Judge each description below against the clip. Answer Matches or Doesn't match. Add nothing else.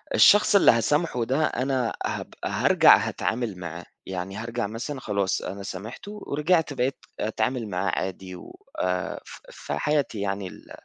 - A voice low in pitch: Matches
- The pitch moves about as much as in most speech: Doesn't match